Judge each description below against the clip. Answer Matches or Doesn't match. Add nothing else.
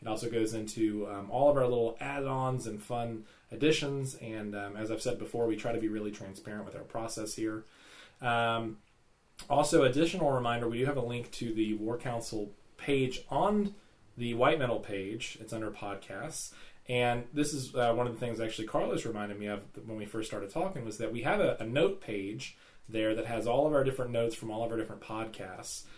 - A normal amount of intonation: Doesn't match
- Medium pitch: Doesn't match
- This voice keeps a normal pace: Doesn't match